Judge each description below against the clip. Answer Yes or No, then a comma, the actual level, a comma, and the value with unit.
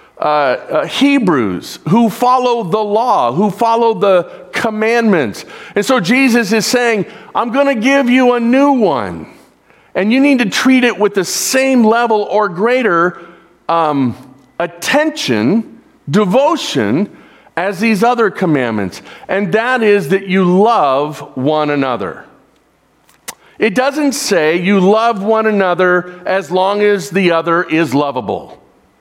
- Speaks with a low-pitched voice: No, high, 210 Hz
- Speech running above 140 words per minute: No, slow, 135 wpm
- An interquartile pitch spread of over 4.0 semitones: Yes, average, 5.2 semitones